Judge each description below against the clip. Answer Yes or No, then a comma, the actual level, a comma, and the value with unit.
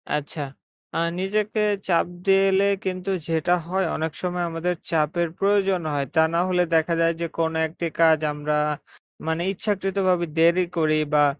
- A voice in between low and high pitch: Yes, medium, 170 Hz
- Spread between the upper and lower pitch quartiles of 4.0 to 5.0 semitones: No, average, 2.8 semitones